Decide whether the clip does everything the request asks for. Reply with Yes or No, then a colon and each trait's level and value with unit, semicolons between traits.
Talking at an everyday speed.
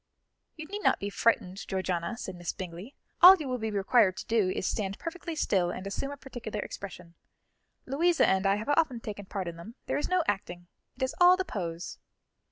No: fast, 210 wpm